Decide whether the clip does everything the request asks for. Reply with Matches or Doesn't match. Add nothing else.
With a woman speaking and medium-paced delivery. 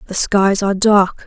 Matches